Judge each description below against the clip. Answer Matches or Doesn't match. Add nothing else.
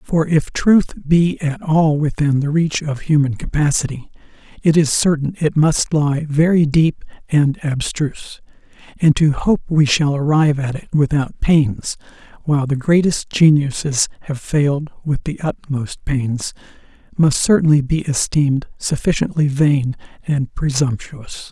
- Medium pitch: Matches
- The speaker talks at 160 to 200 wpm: Doesn't match